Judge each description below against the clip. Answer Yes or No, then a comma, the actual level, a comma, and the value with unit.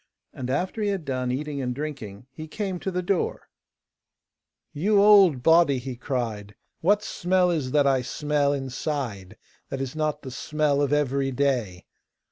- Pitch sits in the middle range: Yes, medium, 145 Hz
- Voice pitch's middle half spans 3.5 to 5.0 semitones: Yes, average, 4.4 semitones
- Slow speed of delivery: No, average, 160 wpm